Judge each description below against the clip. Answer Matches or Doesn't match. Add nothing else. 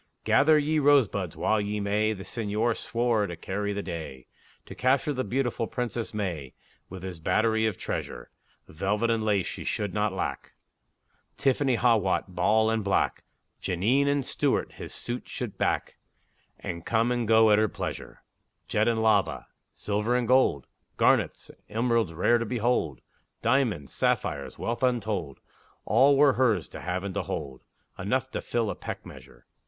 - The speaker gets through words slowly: Doesn't match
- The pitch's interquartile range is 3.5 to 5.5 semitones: Matches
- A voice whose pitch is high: Doesn't match